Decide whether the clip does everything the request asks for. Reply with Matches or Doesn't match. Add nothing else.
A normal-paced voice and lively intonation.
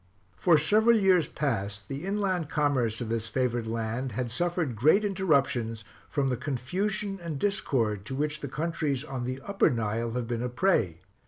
Matches